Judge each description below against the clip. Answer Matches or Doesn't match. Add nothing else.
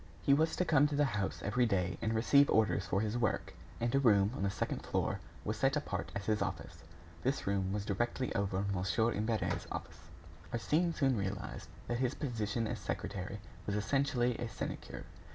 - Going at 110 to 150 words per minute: Doesn't match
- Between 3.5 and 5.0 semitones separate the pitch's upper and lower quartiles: Matches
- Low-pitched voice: Matches